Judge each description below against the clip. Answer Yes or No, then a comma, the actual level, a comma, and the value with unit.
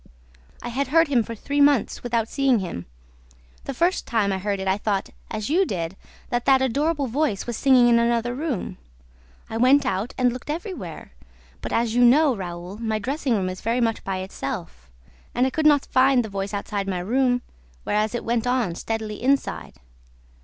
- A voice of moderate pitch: No, high, 235 Hz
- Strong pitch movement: No, average, 4.8 semitones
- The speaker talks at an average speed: Yes, average, 190 wpm